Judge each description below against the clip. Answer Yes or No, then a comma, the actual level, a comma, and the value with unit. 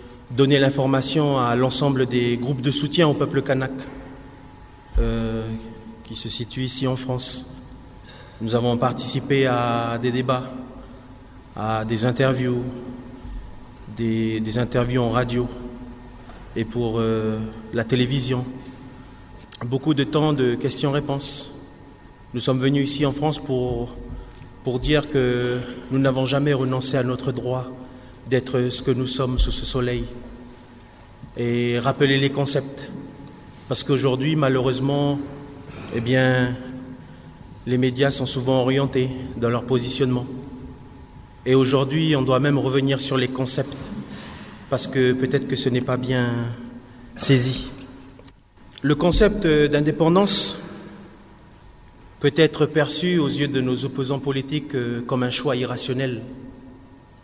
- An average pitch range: No, narrow, 2.0 semitones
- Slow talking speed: Yes, slow, 125 wpm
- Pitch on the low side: Yes, low, 130 Hz